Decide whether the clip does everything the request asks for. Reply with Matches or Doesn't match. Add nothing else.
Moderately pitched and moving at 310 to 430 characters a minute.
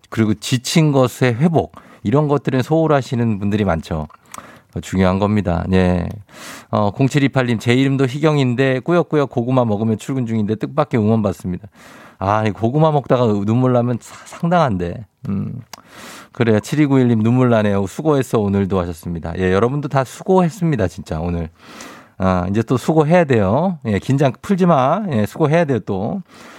Doesn't match